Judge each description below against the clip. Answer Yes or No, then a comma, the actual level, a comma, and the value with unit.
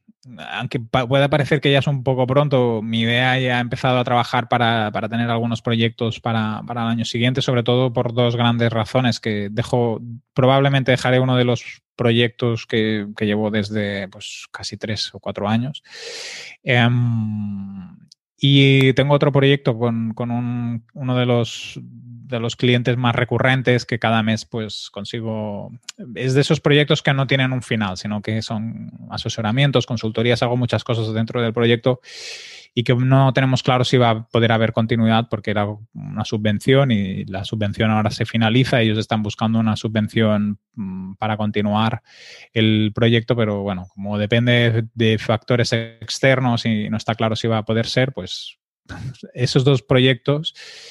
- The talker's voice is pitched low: Yes, low, 120 Hz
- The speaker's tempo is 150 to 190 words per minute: Yes, average, 165 wpm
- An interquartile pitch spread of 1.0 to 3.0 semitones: Yes, narrow, 2.6 semitones